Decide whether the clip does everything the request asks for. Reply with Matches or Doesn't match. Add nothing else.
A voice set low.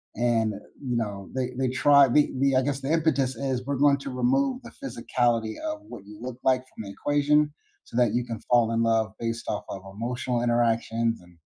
Matches